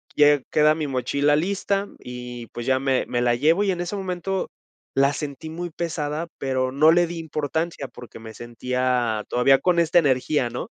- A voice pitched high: No, medium, 145 Hz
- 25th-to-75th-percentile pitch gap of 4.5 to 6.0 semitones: Yes, average, 4.8 semitones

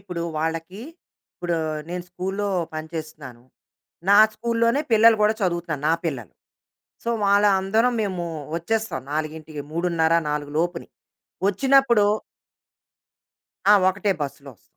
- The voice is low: No, medium, 175 Hz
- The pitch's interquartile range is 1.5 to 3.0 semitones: No, average, 4.7 semitones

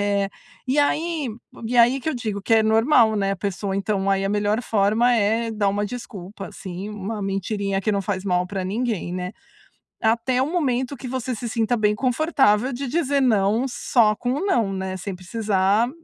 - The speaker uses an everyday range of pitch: Yes, average, 3.9 semitones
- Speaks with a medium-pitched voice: No, high, 215 Hz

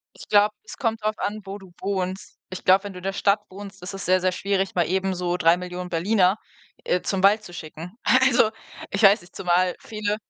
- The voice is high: Yes, high, 195 Hz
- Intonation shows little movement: Yes, narrow, 2.2 semitones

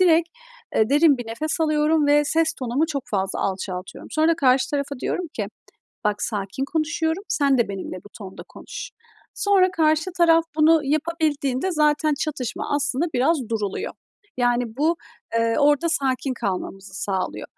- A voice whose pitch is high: Yes, very high, 290 Hz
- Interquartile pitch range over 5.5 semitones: No, average, 5.1 semitones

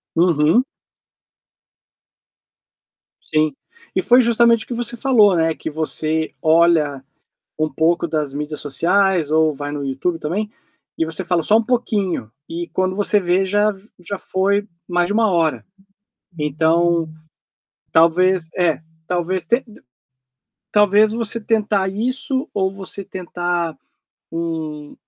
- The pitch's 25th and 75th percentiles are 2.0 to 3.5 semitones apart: No, average, 4.5 semitones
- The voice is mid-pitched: Yes, medium, 175 Hz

